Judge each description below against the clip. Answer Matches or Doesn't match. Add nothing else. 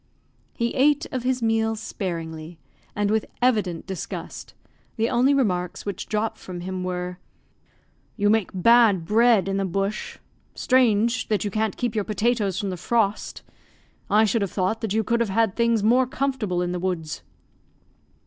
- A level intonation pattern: Doesn't match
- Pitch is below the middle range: Doesn't match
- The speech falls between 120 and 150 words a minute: Doesn't match